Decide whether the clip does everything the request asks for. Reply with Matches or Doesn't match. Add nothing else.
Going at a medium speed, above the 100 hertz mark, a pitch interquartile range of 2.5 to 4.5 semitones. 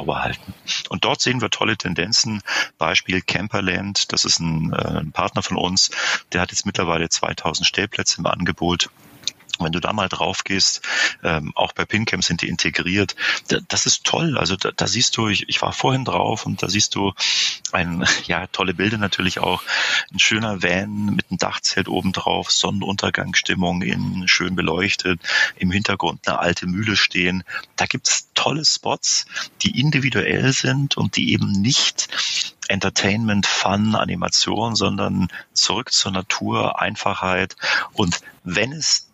Doesn't match